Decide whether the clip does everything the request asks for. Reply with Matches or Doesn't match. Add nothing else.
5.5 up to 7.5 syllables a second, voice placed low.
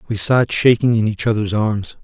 Doesn't match